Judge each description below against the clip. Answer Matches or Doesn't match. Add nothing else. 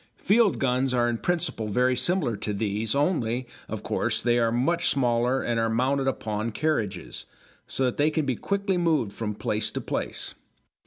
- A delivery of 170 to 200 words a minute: Matches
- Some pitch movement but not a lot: Matches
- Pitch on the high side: Doesn't match